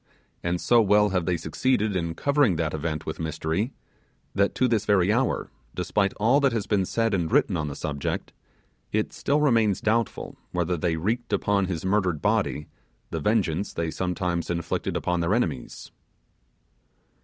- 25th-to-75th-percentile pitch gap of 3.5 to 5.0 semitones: Yes, average, 4.6 semitones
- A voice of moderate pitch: No, very low, 95 Hz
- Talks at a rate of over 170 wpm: No, average, 165 wpm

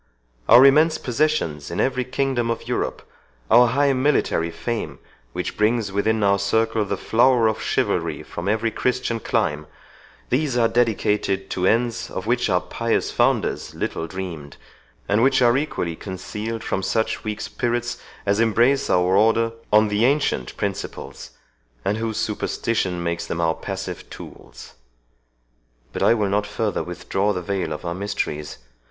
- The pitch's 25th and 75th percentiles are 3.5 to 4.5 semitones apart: Yes, average, 4.0 semitones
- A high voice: No, low, 110 Hz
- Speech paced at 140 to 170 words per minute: Yes, average, 150 wpm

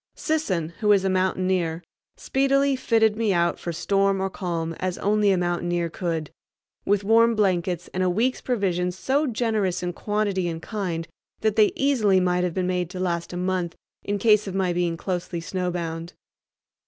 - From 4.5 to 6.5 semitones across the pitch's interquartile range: No, average, 3.2 semitones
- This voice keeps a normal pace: Yes, average, 175 wpm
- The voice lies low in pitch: No, medium, 185 Hz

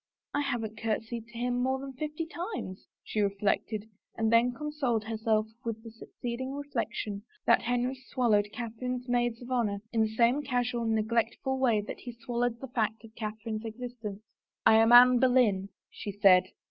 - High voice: Yes, high, 235 Hz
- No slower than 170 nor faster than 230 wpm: Yes, average, 175 wpm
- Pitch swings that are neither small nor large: No, narrow, 2.3 semitones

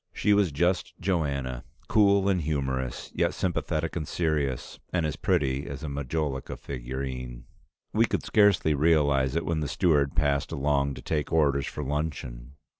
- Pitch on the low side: Yes, very low, 75 Hz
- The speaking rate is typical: Yes, average, 155 wpm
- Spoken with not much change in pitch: No, average, 3.5 semitones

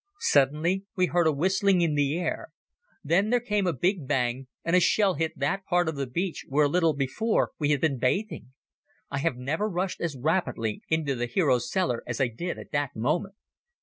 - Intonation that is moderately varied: Yes, average, 5.0 semitones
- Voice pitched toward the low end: No, medium, 160 Hz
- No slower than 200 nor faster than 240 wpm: Yes, fast, 205 wpm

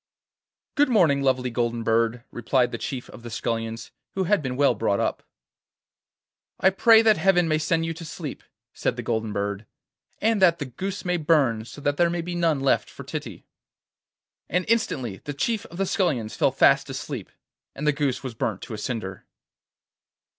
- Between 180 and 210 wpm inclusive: Yes, average, 185 wpm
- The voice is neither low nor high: Yes, medium, 145 Hz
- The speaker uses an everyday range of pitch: No, wide, 7.0 semitones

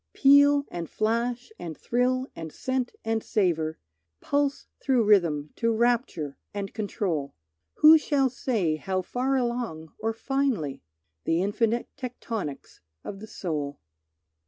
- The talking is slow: Yes, slow, 125 wpm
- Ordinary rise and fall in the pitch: No, wide, 7.1 semitones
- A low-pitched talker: No, high, 225 Hz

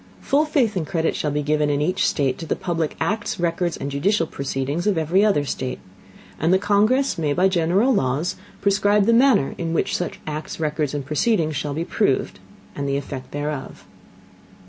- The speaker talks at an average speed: Yes, average, 190 wpm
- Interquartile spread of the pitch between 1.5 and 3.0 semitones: No, average, 5.3 semitones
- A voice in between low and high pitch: Yes, medium, 165 Hz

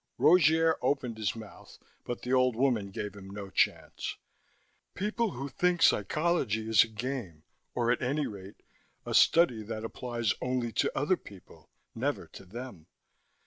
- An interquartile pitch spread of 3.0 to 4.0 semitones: No, average, 4.7 semitones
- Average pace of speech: Yes, average, 150 wpm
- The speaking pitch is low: Yes, low, 120 Hz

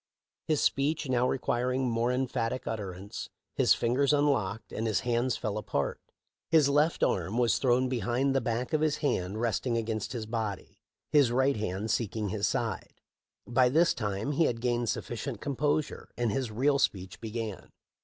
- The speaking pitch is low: Yes, low, 120 Hz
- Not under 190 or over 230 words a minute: No, average, 165 wpm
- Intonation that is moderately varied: Yes, average, 3.7 semitones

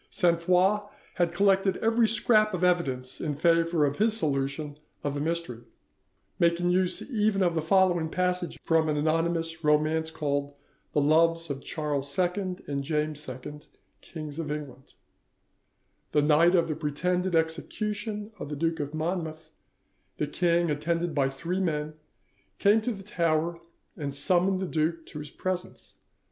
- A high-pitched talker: No, medium, 165 Hz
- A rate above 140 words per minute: Yes, average, 155 wpm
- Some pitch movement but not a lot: Yes, average, 3.2 semitones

